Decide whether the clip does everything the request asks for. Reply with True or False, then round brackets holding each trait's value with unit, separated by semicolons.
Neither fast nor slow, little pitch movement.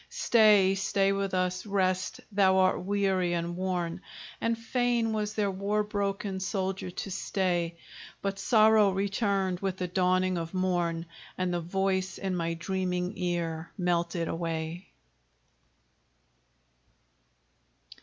False (120 wpm; 1.9 semitones)